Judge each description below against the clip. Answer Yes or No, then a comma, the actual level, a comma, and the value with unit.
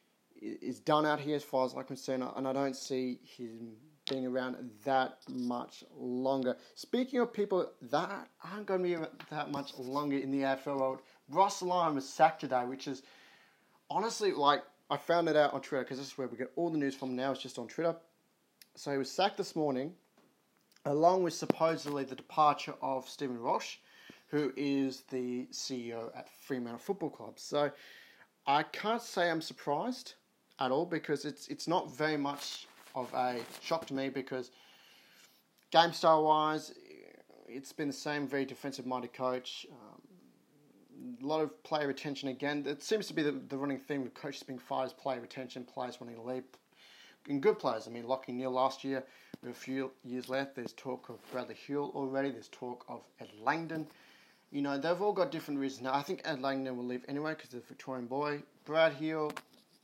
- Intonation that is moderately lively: Yes, average, 3.7 semitones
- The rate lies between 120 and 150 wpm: No, average, 190 wpm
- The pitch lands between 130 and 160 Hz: Yes, medium, 140 Hz